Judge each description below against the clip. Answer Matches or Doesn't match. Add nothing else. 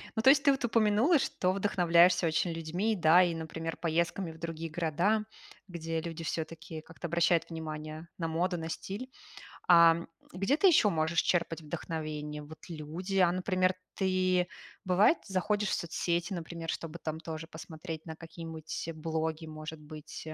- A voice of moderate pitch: Matches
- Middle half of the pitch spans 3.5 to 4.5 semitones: Doesn't match